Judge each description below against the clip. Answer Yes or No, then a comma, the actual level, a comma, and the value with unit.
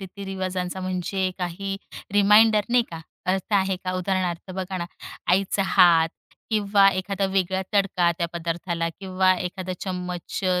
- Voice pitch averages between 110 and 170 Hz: No, medium, 185 Hz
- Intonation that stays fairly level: Yes, narrow, 1.5 semitones